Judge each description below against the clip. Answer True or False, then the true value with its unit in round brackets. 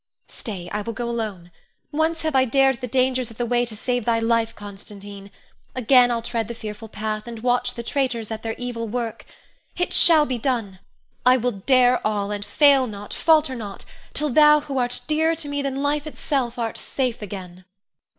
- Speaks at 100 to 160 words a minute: False (195 wpm)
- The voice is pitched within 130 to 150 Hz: False (240 Hz)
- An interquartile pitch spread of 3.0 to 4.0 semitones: True (3.6 semitones)